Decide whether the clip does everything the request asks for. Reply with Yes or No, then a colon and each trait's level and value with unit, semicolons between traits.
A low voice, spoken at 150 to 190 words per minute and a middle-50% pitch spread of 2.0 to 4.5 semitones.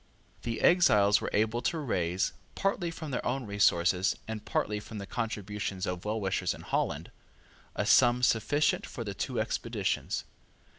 Yes: low, 110 Hz; average, 155 wpm; average, 3.5 semitones